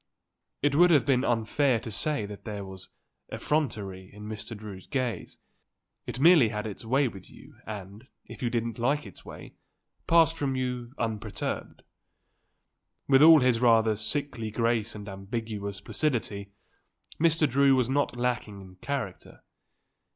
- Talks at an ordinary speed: Yes, average, 145 wpm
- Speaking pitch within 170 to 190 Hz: No, low, 115 Hz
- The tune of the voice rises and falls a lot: No, average, 4.6 semitones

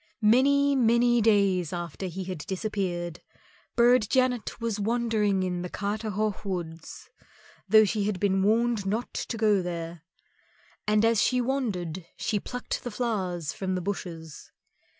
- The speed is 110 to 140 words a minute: Yes, slow, 135 wpm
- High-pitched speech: Yes, high, 205 Hz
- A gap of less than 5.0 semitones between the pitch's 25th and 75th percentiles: Yes, average, 4.1 semitones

